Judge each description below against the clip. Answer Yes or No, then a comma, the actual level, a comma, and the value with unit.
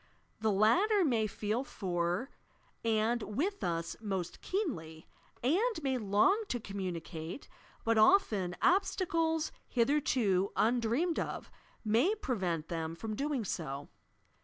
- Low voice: No, high, 225 Hz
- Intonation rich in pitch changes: Yes, wide, 8.4 semitones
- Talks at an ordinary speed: No, slow, 115 wpm